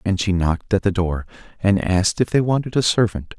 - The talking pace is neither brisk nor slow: No, fast, 230 wpm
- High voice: No, low, 100 Hz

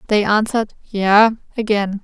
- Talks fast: No, slow, 120 wpm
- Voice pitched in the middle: No, high, 210 Hz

